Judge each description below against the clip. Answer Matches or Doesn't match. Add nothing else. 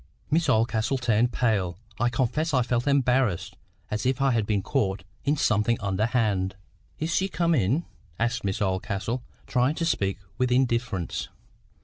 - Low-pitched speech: Matches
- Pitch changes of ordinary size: Matches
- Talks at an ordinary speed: Matches